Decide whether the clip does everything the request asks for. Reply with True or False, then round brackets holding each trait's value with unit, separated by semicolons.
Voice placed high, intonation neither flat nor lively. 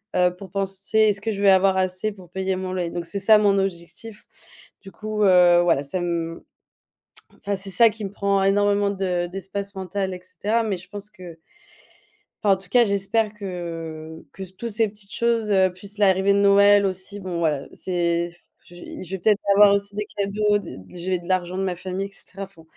False (195 Hz; 2.1 semitones)